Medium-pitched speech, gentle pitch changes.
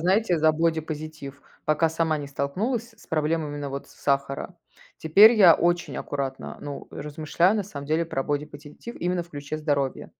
No: medium, 155 Hz; average, 3.1 semitones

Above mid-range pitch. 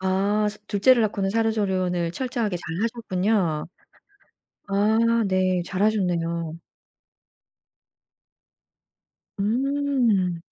Yes: high, 200 Hz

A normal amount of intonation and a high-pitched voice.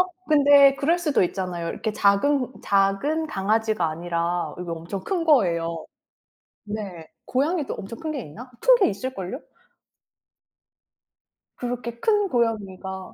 No: wide, 7.4 semitones; high, 220 Hz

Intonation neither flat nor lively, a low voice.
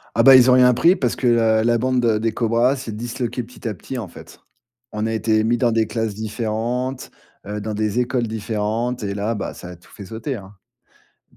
No: narrow, 2.3 semitones; low, 115 Hz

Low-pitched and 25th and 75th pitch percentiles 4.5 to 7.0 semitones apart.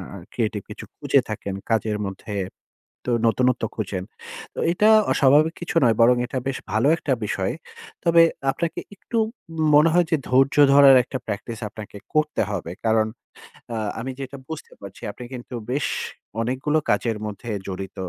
Yes: low, 125 Hz; average, 5.1 semitones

